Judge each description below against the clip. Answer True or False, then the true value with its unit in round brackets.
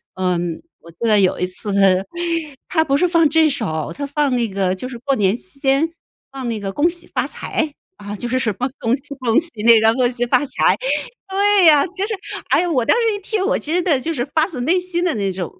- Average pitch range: False (7.3 semitones)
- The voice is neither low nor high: False (260 Hz)